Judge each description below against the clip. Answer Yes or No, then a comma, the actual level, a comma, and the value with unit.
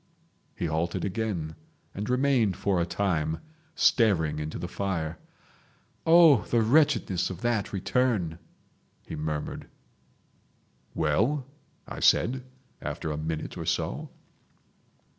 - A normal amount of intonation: No, wide, 7.0 semitones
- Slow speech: Yes, slow, 110 wpm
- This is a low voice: Yes, very low, 95 Hz